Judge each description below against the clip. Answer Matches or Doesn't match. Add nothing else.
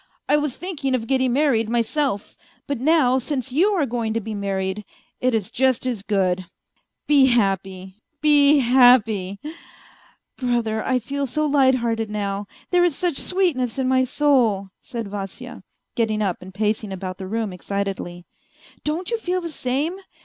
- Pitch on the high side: Matches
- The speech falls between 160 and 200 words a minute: Matches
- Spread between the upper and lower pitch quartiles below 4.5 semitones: Doesn't match